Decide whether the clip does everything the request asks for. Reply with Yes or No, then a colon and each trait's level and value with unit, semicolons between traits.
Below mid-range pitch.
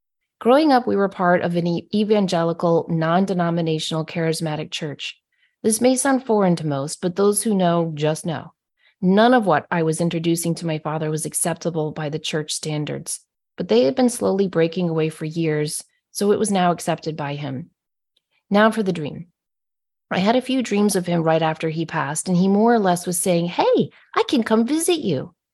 No: medium, 170 Hz